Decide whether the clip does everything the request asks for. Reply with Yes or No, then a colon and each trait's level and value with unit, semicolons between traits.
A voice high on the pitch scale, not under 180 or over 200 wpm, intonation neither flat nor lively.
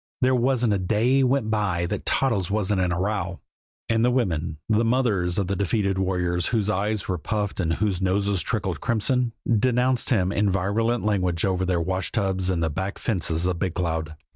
No: low, 100 Hz; average, 190 wpm; average, 3.8 semitones